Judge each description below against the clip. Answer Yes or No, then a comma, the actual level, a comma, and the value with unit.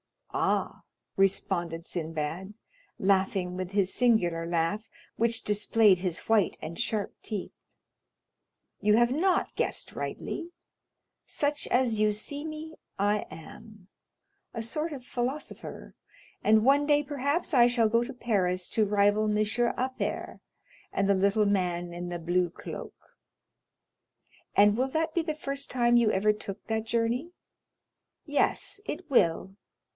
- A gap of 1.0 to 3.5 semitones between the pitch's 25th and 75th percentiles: No, average, 5.0 semitones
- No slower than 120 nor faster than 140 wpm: Yes, slow, 135 wpm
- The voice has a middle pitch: No, high, 215 Hz